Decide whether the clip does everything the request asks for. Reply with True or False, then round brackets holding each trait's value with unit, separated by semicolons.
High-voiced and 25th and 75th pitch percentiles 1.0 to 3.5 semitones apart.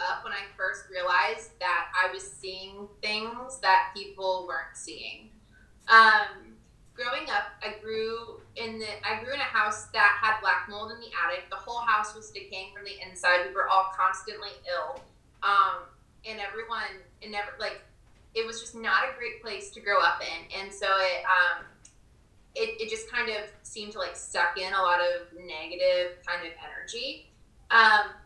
True (200 Hz; 3.2 semitones)